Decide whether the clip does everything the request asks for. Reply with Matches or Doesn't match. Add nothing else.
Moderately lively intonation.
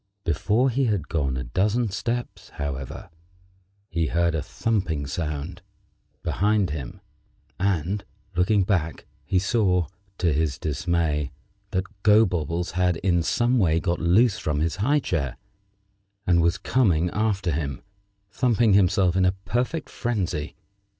Matches